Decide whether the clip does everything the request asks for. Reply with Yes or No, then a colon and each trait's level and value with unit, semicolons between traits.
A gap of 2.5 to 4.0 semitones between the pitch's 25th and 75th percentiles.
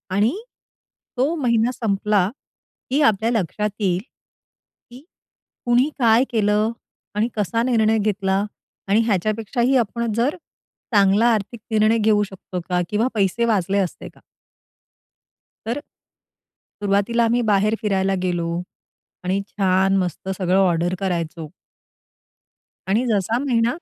Yes: average, 3.2 semitones